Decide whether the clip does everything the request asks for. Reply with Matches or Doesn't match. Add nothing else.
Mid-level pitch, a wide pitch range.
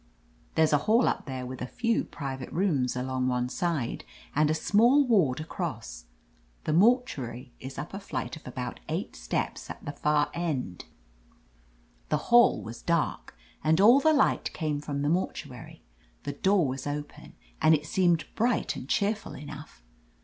Matches